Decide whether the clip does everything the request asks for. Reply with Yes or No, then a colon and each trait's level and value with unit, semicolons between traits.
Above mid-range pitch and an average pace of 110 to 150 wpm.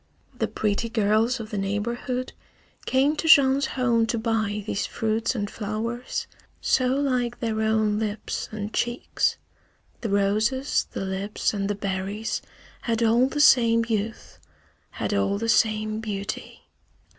Yes: high, 220 Hz; average, 140 wpm